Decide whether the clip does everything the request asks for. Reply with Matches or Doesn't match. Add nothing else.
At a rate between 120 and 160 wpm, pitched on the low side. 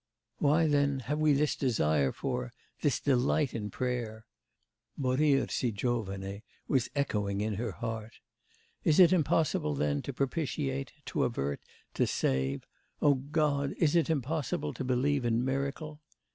Matches